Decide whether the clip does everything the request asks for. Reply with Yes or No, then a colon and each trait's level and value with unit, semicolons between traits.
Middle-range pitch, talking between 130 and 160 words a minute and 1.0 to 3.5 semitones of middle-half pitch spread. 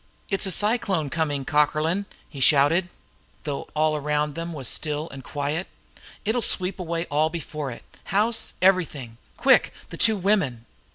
No: medium, 155 Hz; average, 145 wpm; average, 4.3 semitones